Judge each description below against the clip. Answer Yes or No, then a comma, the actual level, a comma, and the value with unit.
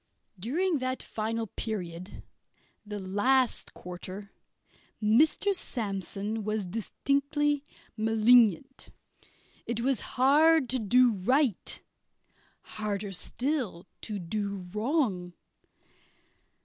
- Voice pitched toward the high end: Yes, high, 225 Hz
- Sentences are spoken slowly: Yes, slow, 85 wpm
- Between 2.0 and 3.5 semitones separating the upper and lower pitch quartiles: No, average, 4.8 semitones